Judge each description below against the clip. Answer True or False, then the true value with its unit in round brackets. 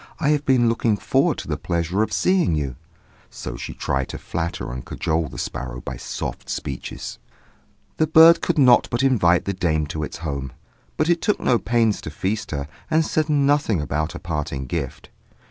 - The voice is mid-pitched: False (90 Hz)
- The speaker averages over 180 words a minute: True (190 wpm)